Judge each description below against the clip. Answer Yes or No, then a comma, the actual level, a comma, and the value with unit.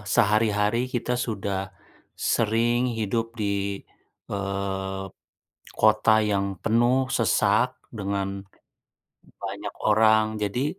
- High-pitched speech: No, low, 105 Hz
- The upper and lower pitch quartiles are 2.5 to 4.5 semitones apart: Yes, average, 2.8 semitones